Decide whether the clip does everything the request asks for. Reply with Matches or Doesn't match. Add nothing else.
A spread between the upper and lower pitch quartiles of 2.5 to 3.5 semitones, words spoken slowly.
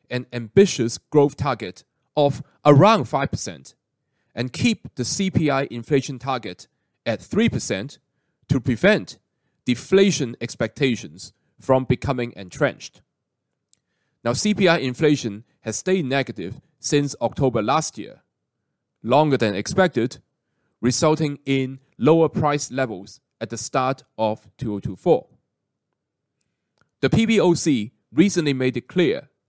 Doesn't match